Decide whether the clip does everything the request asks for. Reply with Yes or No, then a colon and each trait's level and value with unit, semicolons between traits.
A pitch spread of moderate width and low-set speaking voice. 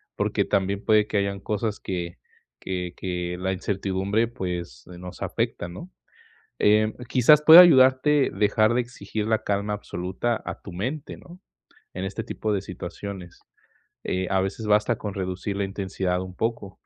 Yes: average, 3.0 semitones; low, 100 Hz